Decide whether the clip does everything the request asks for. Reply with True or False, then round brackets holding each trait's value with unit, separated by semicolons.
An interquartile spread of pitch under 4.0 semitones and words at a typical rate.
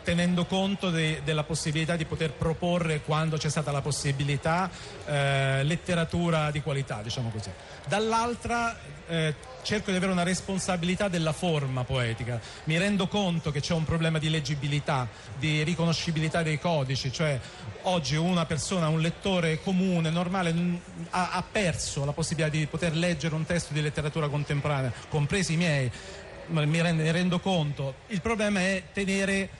True (3.2 semitones; 155 wpm)